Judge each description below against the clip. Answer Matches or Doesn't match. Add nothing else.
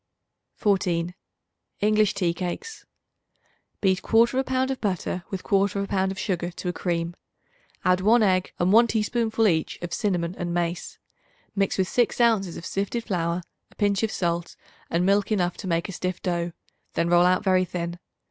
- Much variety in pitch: Doesn't match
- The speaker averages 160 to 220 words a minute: Matches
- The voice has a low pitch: Doesn't match